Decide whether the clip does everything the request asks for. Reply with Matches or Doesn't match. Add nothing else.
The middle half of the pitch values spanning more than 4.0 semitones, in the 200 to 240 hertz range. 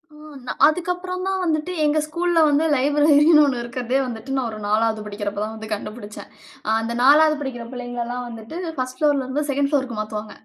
Doesn't match